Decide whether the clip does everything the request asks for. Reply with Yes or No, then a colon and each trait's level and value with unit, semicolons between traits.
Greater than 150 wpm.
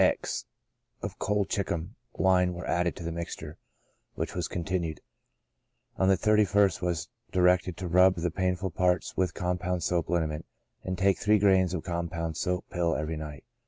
Yes: average, 165 wpm